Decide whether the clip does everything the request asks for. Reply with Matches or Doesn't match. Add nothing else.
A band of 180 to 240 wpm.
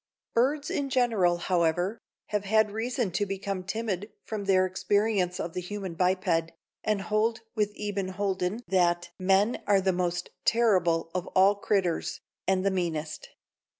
Doesn't match